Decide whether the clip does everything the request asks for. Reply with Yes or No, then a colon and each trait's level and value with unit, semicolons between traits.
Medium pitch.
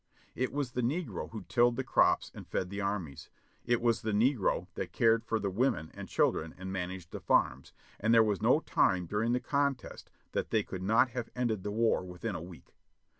No: low, 110 Hz